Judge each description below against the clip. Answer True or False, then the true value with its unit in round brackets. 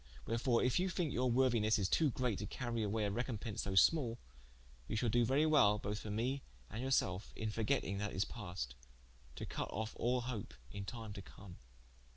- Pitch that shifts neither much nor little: True (3.6 semitones)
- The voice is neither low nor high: False (115 Hz)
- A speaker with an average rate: True (190 wpm)